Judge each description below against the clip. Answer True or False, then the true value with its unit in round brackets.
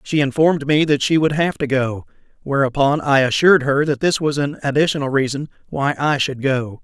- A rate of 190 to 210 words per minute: True (200 wpm)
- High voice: False (140 Hz)